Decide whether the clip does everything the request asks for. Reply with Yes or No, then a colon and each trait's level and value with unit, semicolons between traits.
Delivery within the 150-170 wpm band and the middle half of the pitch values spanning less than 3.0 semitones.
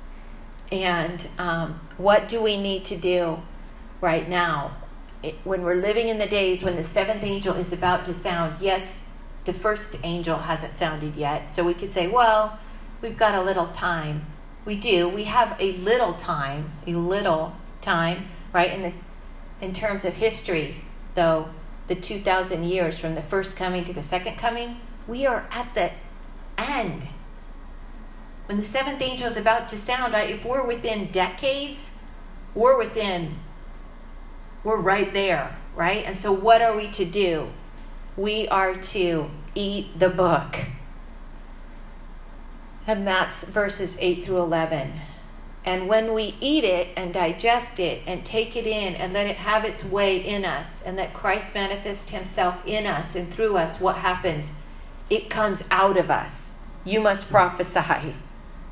No: average, 155 wpm; average, 3.5 semitones